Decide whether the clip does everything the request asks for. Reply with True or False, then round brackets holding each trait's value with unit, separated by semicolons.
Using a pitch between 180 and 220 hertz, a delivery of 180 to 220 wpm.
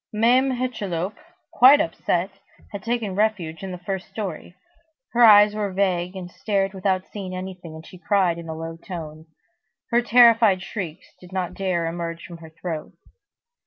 False (185 Hz; 165 wpm)